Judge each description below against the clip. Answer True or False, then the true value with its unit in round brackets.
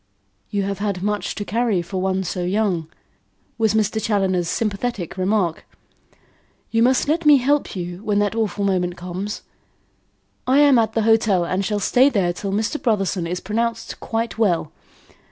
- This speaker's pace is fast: False (165 wpm)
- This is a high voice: True (205 Hz)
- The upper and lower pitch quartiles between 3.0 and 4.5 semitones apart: True (3.4 semitones)